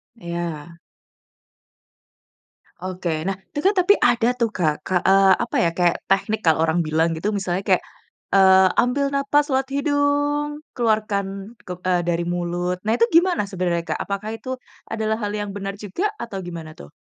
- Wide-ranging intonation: Yes, wide, 5.7 semitones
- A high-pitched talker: Yes, high, 195 Hz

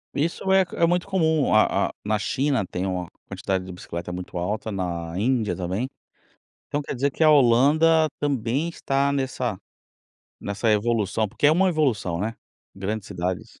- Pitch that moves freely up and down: Yes, wide, 7.3 semitones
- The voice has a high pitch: No, low, 115 Hz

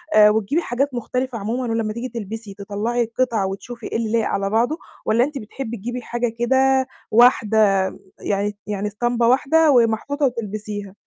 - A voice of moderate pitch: No, high, 230 Hz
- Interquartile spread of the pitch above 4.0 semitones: No, average, 3.0 semitones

